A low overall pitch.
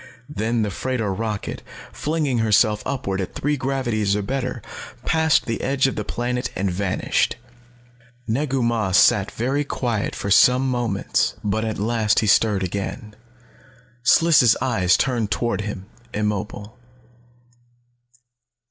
Yes: low, 115 Hz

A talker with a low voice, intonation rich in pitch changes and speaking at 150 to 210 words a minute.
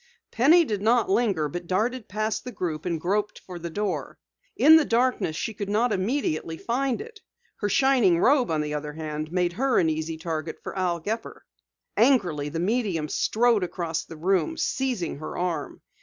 No: high, 190 Hz; wide, 6.7 semitones; average, 180 wpm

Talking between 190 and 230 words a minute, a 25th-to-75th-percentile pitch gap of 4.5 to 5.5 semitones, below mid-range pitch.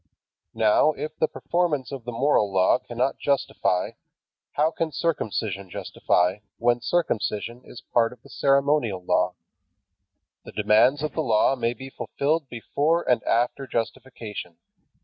No: slow, 135 wpm; average, 4.8 semitones; low, 125 Hz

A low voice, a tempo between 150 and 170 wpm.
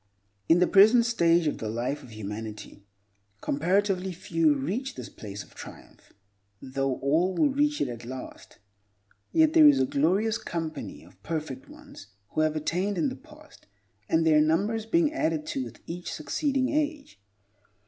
No: medium, 165 Hz; average, 160 wpm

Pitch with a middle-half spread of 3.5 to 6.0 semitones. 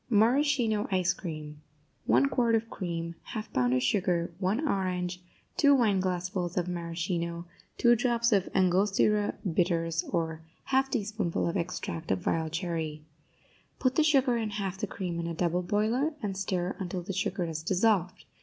Yes: average, 4.2 semitones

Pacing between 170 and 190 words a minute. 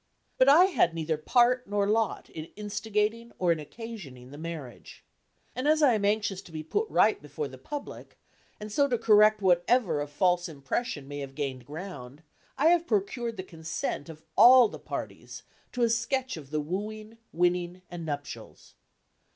Yes: average, 175 wpm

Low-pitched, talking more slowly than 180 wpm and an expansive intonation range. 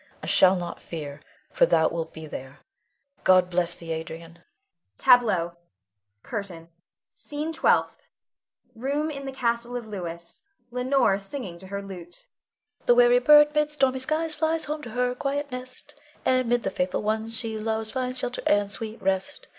No: high, 225 Hz; average, 160 wpm; wide, 7.0 semitones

